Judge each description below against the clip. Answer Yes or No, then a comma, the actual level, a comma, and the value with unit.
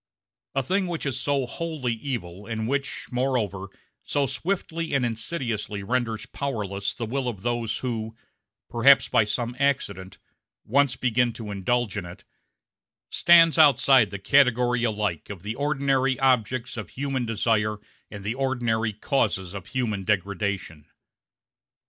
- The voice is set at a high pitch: No, low, 120 Hz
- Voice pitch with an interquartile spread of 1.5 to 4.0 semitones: No, average, 4.4 semitones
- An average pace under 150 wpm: Yes, slow, 135 wpm